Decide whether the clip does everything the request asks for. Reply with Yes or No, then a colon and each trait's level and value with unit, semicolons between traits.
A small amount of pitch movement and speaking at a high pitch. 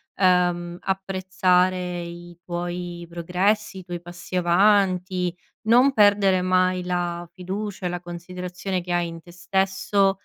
No: narrow, 1.6 semitones; medium, 180 Hz